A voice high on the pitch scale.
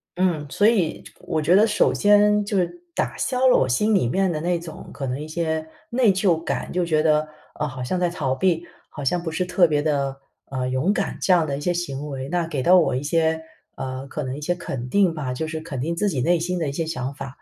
No: medium, 160 Hz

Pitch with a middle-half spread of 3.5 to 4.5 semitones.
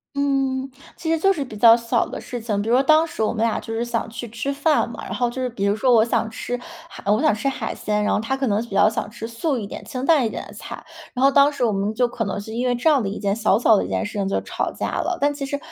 Yes: average, 3.9 semitones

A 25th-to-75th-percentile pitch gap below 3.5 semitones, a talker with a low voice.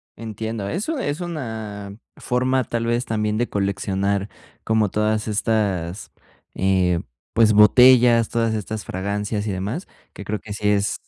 Yes: narrow, 2.5 semitones; low, 105 Hz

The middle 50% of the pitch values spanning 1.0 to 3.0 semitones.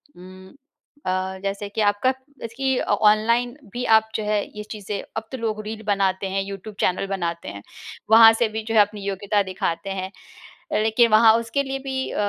Yes: average, 2.7 semitones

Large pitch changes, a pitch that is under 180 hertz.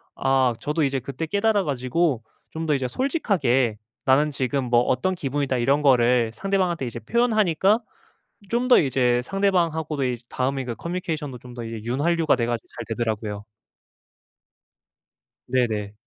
Yes: wide, 5.7 semitones; low, 135 Hz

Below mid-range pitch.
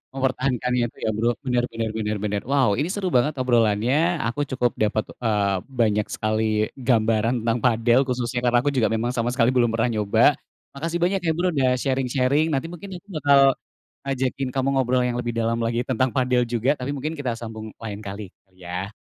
Yes: low, 120 Hz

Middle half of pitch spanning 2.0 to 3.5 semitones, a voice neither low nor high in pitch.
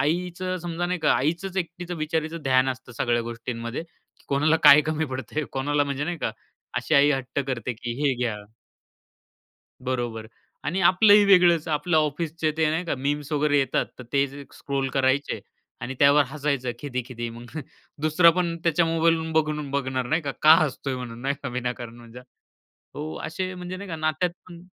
No: average, 4.2 semitones; medium, 145 Hz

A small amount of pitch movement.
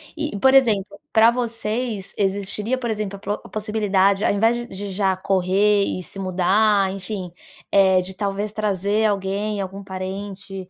Yes: narrow, 1.9 semitones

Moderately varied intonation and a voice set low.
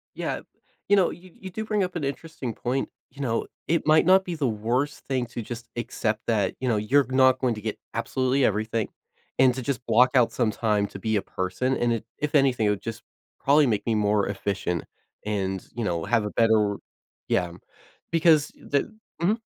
Yes: average, 4.8 semitones; low, 120 Hz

